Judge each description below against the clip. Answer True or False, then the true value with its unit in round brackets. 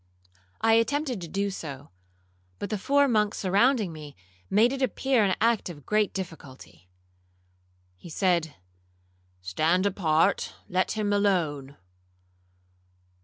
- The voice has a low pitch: False (195 Hz)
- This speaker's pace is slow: True (115 wpm)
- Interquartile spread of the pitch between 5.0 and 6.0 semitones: True (5.4 semitones)